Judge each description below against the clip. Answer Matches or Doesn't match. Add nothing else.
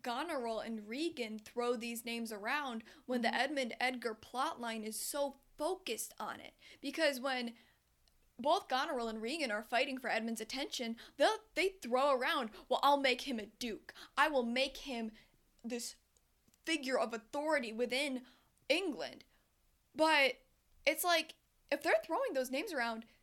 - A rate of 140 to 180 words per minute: Matches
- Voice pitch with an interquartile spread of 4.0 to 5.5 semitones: Doesn't match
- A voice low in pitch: Doesn't match